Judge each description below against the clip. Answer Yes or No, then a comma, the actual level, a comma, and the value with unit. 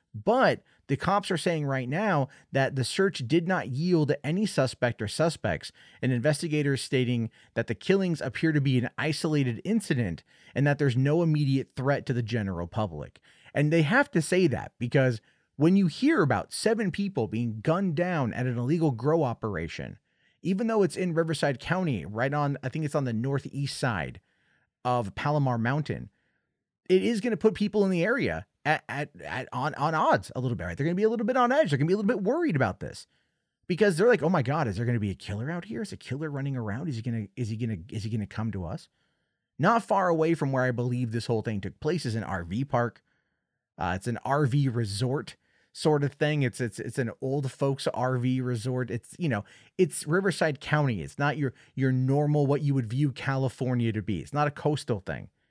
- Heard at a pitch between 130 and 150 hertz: Yes, medium, 140 Hz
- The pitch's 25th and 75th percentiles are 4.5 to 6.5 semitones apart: Yes, average, 5.2 semitones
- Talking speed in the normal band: No, fast, 225 wpm